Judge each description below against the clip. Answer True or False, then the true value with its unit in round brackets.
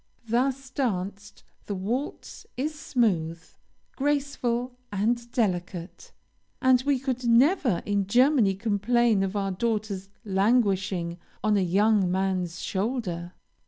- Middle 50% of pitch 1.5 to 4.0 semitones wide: False (4.5 semitones)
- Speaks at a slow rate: True (110 wpm)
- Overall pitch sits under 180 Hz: False (215 Hz)